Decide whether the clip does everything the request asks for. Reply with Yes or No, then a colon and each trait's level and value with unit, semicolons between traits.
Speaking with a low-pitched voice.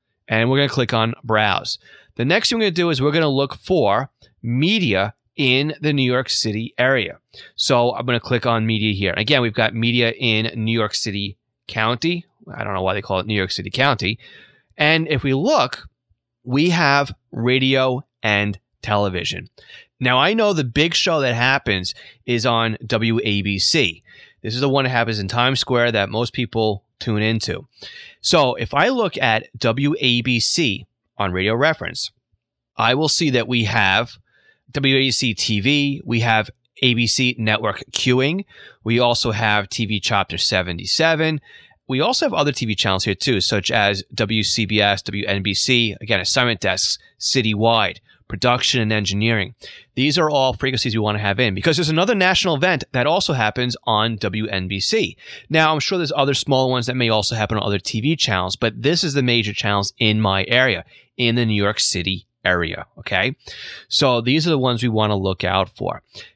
Yes: low, 115 Hz